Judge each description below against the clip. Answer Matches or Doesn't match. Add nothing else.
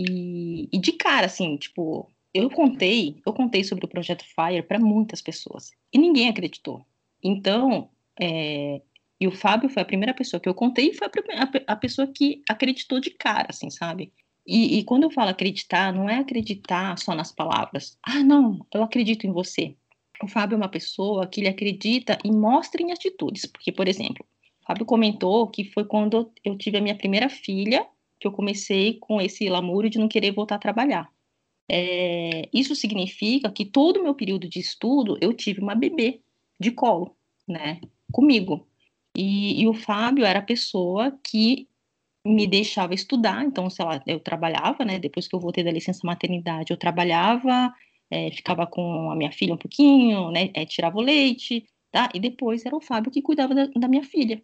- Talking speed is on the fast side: Matches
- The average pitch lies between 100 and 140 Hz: Doesn't match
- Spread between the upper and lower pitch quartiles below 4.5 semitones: Doesn't match